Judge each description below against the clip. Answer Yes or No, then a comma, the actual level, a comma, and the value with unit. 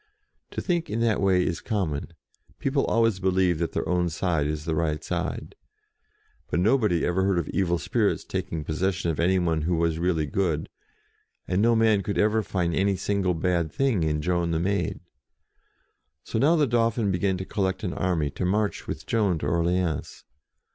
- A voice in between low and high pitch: No, very low, 90 Hz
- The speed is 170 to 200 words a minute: Yes, average, 180 wpm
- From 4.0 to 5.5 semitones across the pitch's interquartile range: No, average, 3.4 semitones